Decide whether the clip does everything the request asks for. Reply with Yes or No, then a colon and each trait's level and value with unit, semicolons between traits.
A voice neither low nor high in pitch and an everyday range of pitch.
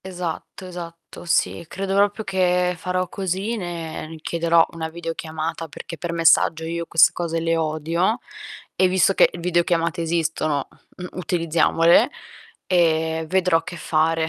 No: medium, 170 Hz; narrow, 1.7 semitones